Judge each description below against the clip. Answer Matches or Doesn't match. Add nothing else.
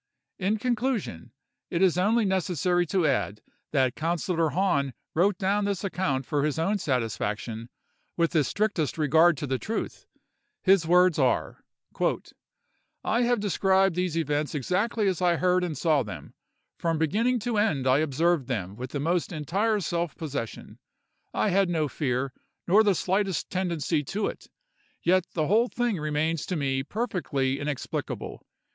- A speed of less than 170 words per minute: Matches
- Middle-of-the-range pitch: Matches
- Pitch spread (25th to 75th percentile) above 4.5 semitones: Matches